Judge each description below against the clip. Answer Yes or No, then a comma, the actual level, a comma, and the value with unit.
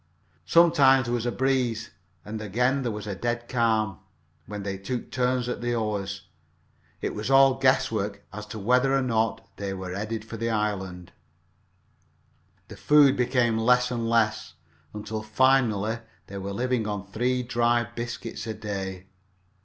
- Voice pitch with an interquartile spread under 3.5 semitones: Yes, average, 3.0 semitones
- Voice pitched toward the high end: No, low, 115 Hz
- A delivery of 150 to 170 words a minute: Yes, average, 160 wpm